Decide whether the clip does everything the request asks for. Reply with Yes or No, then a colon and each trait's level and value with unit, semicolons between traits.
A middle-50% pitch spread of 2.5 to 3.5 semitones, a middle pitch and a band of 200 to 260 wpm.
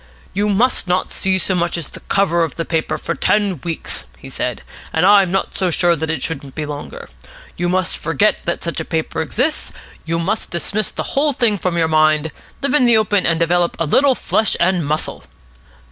No: average, 4.0 semitones; medium, 175 Hz; fast, 205 wpm